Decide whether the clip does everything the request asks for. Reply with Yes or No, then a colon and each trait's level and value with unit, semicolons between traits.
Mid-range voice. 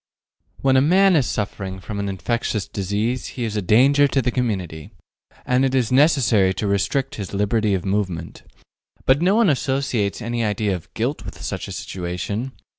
No: low, 110 Hz